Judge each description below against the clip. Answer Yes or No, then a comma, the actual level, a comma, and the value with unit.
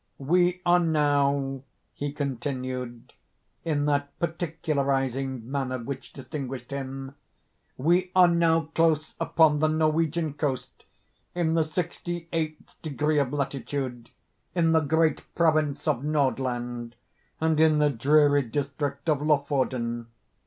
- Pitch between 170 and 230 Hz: No, medium, 145 Hz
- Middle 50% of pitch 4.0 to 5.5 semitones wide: No, average, 3.0 semitones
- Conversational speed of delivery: No, slow, 105 wpm